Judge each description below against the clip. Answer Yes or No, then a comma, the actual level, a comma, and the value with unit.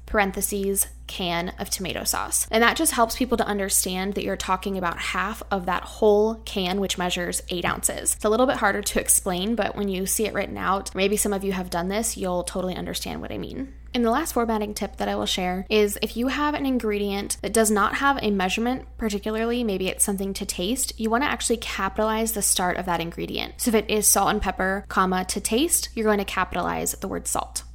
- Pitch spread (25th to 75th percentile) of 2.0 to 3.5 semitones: Yes, average, 3.0 semitones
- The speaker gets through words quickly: Yes, fast, 225 wpm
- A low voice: No, high, 205 Hz